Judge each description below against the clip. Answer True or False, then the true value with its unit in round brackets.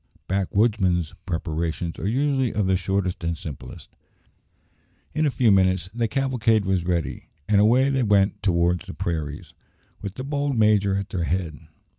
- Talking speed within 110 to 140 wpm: False (155 wpm)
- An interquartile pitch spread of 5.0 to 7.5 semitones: False (4.6 semitones)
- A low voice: True (95 Hz)